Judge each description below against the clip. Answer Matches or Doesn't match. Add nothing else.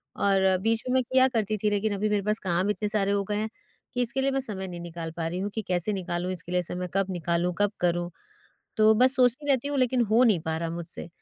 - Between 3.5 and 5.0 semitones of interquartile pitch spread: Matches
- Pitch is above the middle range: Matches